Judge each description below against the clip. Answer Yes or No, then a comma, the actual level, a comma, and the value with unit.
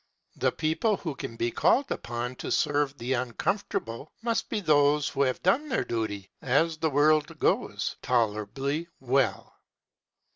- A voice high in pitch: No, medium, 140 Hz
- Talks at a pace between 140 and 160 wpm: Yes, average, 145 wpm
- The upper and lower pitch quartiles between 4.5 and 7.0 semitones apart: Yes, average, 5.0 semitones